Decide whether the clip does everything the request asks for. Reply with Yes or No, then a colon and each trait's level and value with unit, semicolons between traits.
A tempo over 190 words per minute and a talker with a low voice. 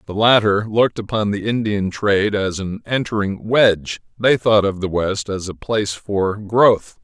No: average, 180 wpm; low, 105 Hz